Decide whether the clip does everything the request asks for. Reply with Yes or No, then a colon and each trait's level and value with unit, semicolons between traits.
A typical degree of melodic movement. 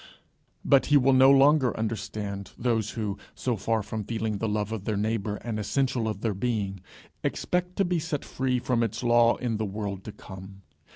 Yes: average, 3.5 semitones